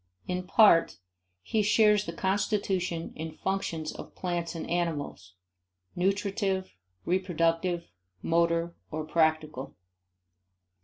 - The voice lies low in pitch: No, medium, 175 Hz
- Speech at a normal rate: No, slow, 95 wpm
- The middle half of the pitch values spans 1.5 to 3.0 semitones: Yes, average, 2.7 semitones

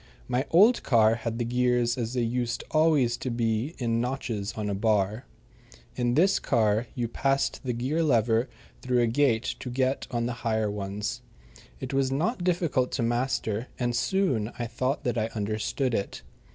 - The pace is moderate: Yes, average, 175 wpm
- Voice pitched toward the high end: No, low, 120 Hz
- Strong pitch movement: No, average, 2.9 semitones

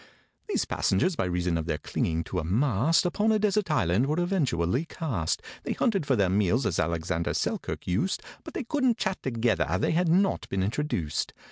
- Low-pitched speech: Yes, low, 120 Hz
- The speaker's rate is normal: Yes, average, 180 wpm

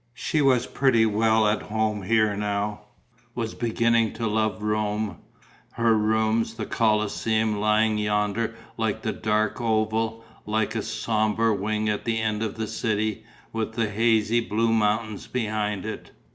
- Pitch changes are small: Yes, narrow, 1.0 semitones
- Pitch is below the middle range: Yes, low, 110 Hz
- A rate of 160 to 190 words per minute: No, average, 145 wpm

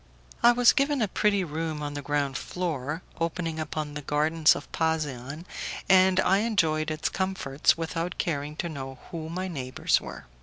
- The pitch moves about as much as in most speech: Yes, average, 3.8 semitones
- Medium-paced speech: Yes, average, 165 wpm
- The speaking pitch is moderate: Yes, medium, 160 Hz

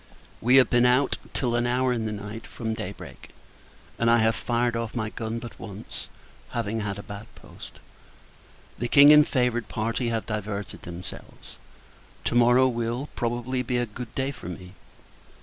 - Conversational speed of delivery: Yes, average, 175 wpm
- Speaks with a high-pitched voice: No, low, 115 Hz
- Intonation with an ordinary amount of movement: No, narrow, 2.0 semitones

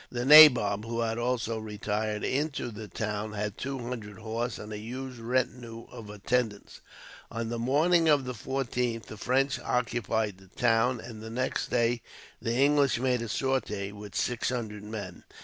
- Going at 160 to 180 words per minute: Yes, average, 165 wpm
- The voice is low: Yes, low, 115 Hz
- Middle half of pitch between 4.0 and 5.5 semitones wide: No, average, 2.9 semitones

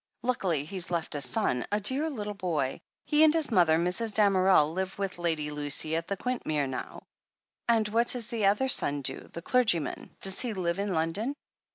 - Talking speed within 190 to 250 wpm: Yes, average, 195 wpm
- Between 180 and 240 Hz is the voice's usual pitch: Yes, high, 190 Hz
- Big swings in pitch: Yes, wide, 5.9 semitones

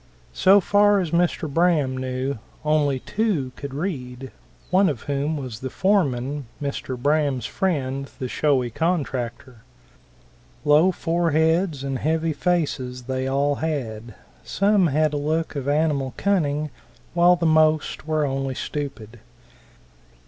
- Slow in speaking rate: Yes, slow, 125 wpm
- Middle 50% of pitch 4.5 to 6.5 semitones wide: No, average, 3.9 semitones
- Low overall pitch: No, medium, 145 Hz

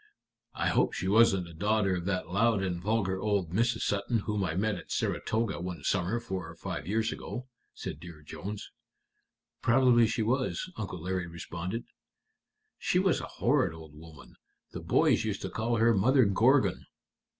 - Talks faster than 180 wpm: No, average, 170 wpm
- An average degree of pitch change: Yes, average, 4.1 semitones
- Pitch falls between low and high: No, low, 100 Hz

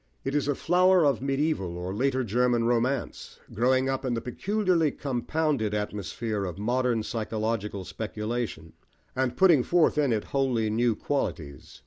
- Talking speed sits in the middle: Yes, average, 145 wpm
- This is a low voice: Yes, low, 120 Hz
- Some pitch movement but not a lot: Yes, average, 4.5 semitones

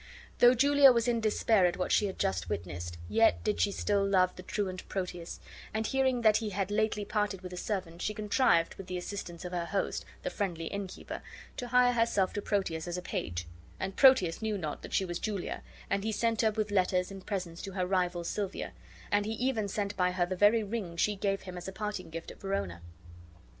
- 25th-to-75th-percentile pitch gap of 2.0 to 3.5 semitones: Yes, average, 3.1 semitones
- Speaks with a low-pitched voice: No, high, 195 Hz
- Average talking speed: No, fast, 215 wpm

